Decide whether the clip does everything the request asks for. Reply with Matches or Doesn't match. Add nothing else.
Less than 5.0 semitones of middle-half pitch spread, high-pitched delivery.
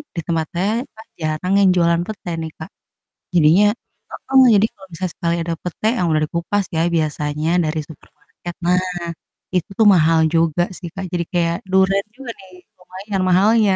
Doesn't match